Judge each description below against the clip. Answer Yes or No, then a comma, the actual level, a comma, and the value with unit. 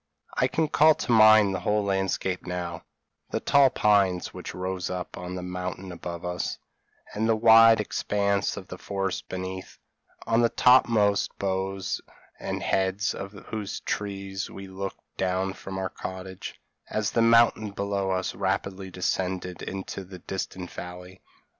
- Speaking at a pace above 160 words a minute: No, average, 145 wpm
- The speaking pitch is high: No, very low, 95 Hz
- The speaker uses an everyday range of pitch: No, narrow, 2.0 semitones